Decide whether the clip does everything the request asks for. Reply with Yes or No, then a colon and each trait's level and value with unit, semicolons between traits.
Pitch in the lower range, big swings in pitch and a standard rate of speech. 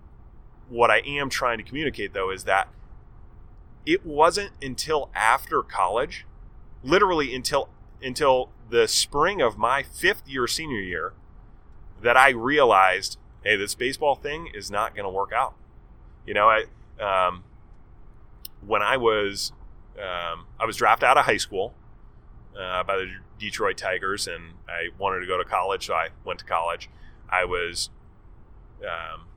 Yes: low, 130 Hz; wide, 7.7 semitones; average, 150 wpm